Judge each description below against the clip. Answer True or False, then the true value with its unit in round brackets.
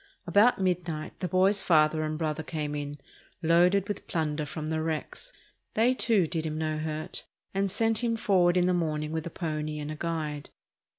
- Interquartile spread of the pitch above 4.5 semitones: False (3.3 semitones)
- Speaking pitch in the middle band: True (160 Hz)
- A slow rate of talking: False (185 wpm)